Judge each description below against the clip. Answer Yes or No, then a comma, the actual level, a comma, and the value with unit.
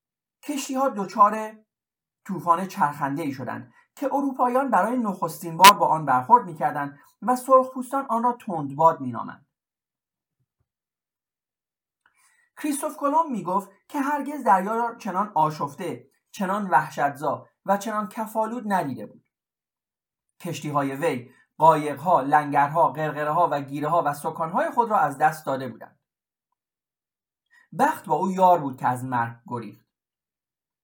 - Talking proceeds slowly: No, average, 130 wpm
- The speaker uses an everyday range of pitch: No, wide, 8.8 semitones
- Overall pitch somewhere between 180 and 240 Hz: Yes, high, 190 Hz